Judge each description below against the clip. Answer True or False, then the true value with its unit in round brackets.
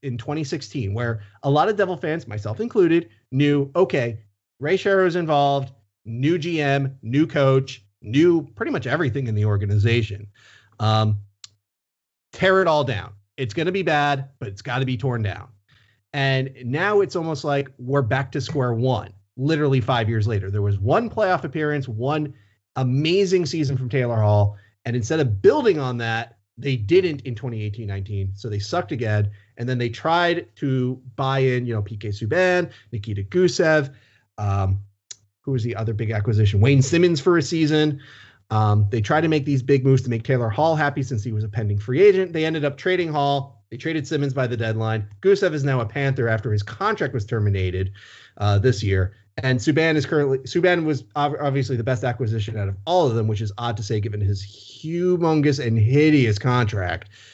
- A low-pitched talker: True (130 Hz)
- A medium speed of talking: True (185 wpm)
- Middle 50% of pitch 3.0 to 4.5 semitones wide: False (5.6 semitones)